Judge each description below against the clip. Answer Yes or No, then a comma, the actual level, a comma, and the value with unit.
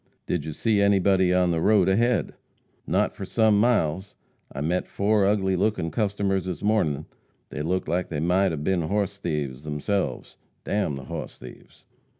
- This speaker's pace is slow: No, average, 170 wpm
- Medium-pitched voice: No, very low, 95 Hz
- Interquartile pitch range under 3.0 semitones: No, average, 3.9 semitones